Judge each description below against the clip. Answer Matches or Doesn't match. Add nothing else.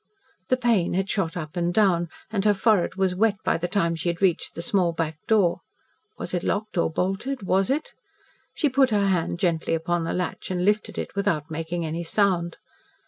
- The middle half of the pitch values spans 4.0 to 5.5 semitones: Doesn't match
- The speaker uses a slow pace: Doesn't match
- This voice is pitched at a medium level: Matches